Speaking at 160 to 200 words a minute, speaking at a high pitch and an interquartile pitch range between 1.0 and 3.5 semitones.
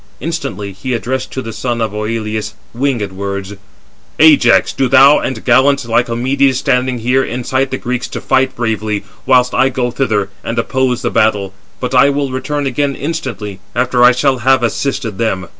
No: average, 170 wpm; low, 125 Hz; average, 3.2 semitones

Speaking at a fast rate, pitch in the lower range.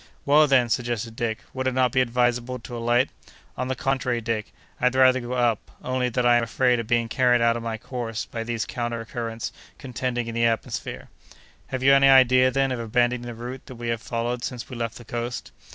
Yes: fast, 215 wpm; low, 120 Hz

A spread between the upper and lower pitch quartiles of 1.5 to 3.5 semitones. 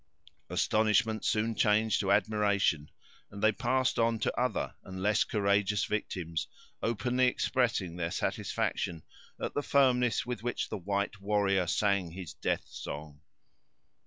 Yes: average, 3.2 semitones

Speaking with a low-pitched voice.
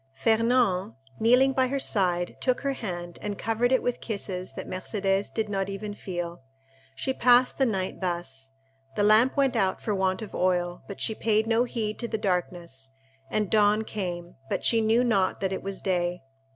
No: high, 205 Hz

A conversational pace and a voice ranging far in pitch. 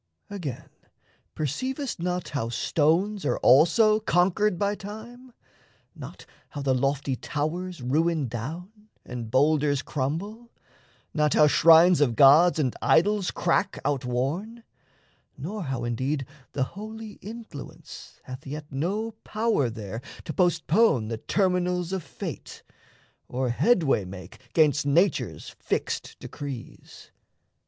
No: slow, 115 wpm; wide, 6.7 semitones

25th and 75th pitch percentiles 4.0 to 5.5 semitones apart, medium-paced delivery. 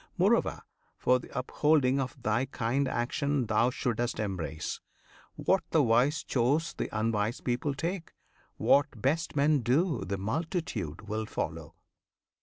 No: average, 4.9 semitones; slow, 130 wpm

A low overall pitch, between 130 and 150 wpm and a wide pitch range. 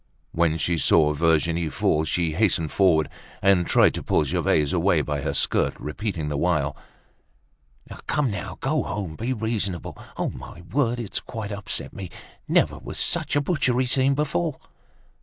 No: very low, 90 Hz; average, 160 wpm; wide, 6.4 semitones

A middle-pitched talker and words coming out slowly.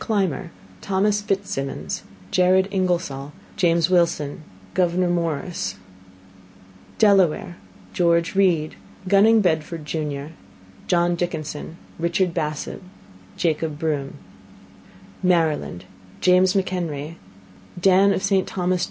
Yes: medium, 175 Hz; slow, 90 wpm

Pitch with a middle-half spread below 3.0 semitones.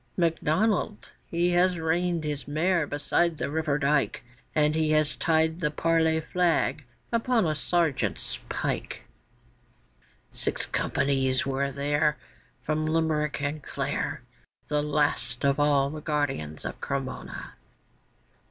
Yes: narrow, 2.4 semitones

